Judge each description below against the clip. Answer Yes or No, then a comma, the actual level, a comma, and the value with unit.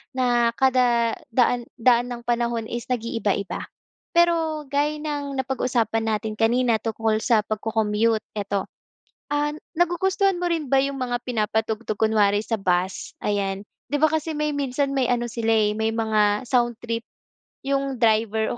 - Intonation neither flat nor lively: Yes, average, 3.8 semitones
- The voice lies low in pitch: No, high, 235 Hz